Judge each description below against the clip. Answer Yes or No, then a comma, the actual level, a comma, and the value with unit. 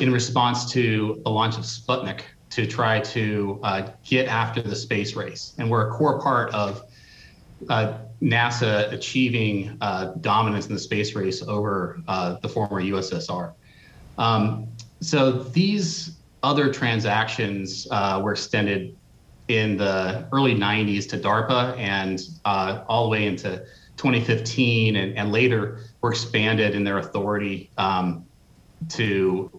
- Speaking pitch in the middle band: No, low, 110 Hz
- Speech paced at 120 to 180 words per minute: Yes, slow, 135 wpm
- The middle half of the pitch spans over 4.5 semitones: No, average, 3.3 semitones